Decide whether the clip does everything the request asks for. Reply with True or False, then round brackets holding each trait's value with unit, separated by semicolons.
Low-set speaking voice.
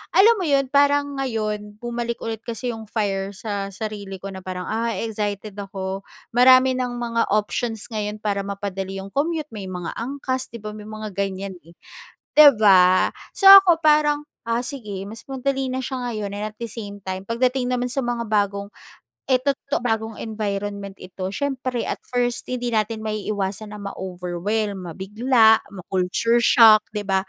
False (215 Hz)